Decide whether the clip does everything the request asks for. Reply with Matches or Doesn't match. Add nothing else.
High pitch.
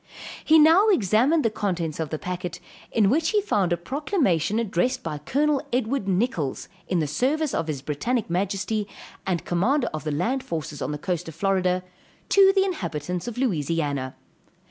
Matches